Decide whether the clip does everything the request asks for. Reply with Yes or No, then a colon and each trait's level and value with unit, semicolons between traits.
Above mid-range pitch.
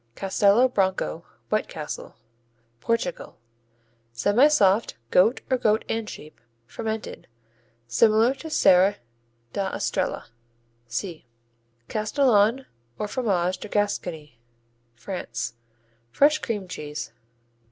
Yes: high, 205 Hz